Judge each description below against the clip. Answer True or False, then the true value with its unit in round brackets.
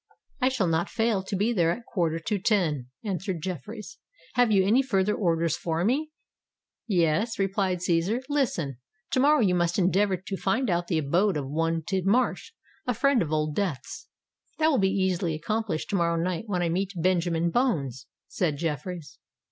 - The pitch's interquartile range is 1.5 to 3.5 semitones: False (4.2 semitones)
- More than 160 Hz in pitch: True (185 Hz)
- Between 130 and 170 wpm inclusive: False (180 wpm)